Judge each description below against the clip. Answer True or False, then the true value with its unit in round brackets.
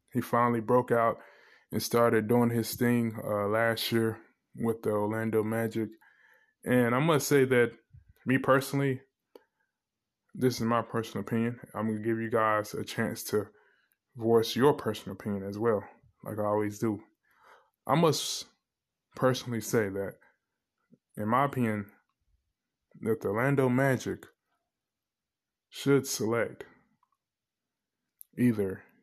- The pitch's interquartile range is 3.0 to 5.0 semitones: False (2.4 semitones)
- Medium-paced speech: False (125 wpm)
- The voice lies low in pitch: True (115 Hz)